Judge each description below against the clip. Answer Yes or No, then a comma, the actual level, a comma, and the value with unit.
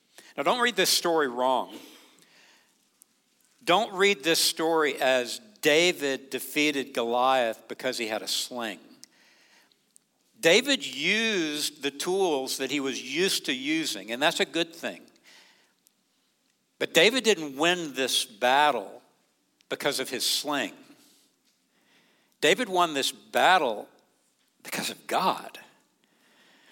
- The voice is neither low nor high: Yes, medium, 165 Hz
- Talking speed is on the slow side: Yes, slow, 115 wpm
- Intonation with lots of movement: Yes, wide, 8.5 semitones